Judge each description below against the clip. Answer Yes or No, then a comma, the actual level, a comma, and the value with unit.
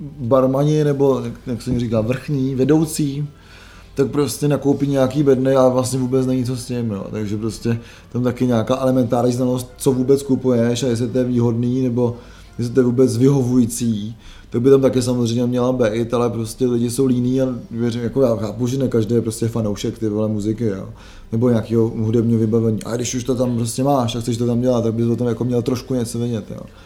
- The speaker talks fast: Yes, fast, 210 wpm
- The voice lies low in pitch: Yes, low, 120 Hz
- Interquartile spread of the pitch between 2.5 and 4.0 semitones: No, narrow, 2.1 semitones